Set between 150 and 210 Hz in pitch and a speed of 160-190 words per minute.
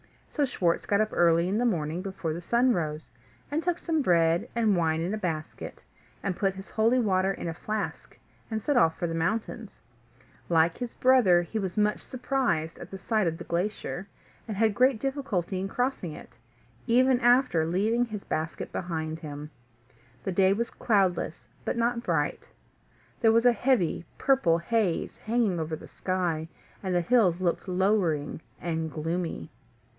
Yes: high, 190 Hz; average, 170 wpm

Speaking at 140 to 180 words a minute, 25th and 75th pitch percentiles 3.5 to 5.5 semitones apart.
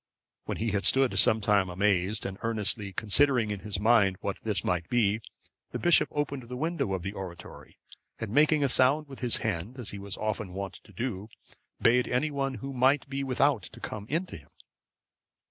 No: average, 195 wpm; average, 5.2 semitones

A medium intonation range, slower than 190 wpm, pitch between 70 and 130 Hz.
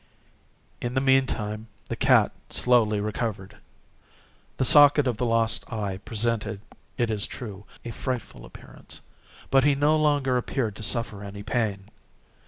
Yes: average, 3.8 semitones; average, 140 wpm; low, 115 Hz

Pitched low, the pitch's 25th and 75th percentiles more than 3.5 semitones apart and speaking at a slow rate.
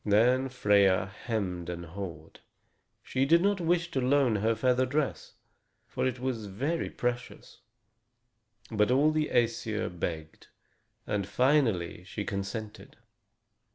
Yes: low, 115 Hz; average, 5.0 semitones; slow, 120 wpm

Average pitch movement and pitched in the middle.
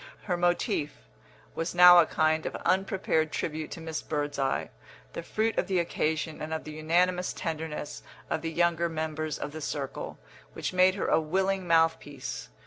No: narrow, 2.2 semitones; medium, 160 Hz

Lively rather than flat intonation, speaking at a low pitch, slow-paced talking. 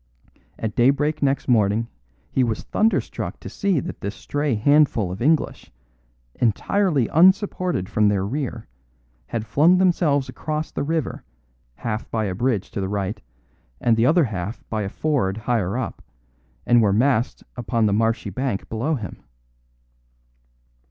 No: wide, 5.7 semitones; low, 120 Hz; average, 145 wpm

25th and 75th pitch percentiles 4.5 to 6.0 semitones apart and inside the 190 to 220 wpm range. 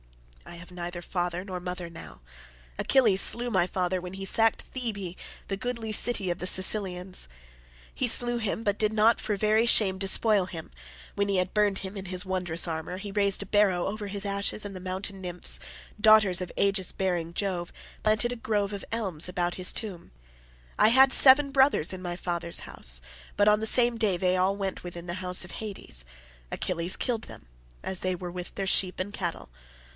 No: average, 2.9 semitones; average, 195 wpm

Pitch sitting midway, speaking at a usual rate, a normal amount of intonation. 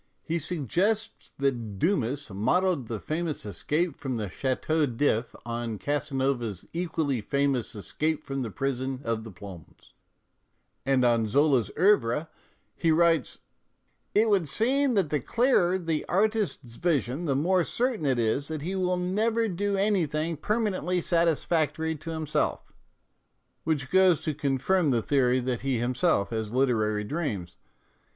No: medium, 145 Hz; average, 145 wpm; wide, 6.3 semitones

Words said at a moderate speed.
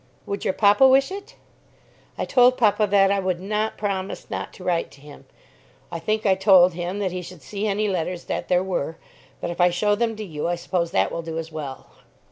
No: fast, 225 wpm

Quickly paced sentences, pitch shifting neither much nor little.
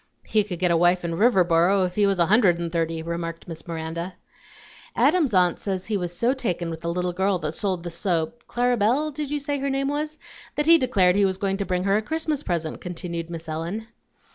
No: fast, 230 wpm; wide, 5.7 semitones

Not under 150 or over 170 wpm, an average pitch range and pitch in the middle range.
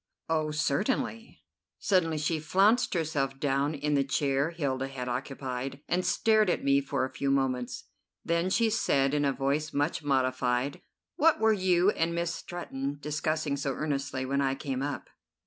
Yes: average, 165 wpm; average, 3.7 semitones; medium, 145 Hz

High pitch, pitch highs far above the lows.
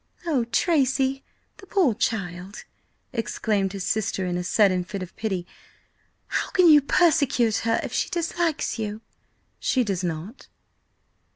Yes: high, 225 Hz; wide, 6.3 semitones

